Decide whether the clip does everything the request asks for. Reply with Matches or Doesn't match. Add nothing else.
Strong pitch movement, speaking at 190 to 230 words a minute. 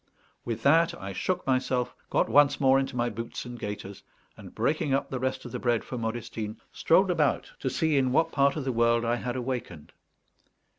Doesn't match